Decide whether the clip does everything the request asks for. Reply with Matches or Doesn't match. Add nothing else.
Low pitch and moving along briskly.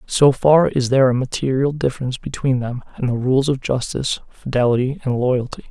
Doesn't match